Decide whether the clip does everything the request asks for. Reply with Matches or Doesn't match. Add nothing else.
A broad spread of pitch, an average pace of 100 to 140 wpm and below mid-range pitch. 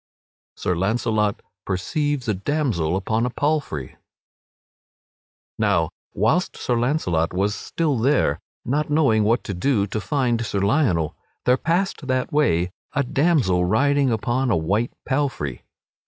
Matches